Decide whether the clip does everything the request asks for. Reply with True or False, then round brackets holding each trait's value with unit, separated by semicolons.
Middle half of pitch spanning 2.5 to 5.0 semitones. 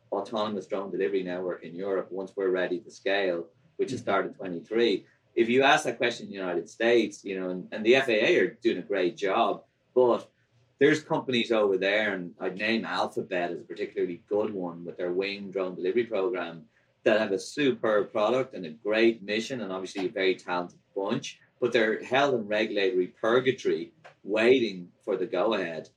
False (5.4 semitones)